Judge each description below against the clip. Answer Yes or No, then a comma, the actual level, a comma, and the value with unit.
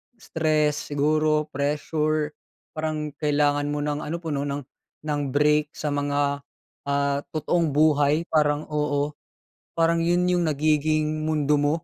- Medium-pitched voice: Yes, medium, 150 Hz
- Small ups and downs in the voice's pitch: Yes, narrow, 1.2 semitones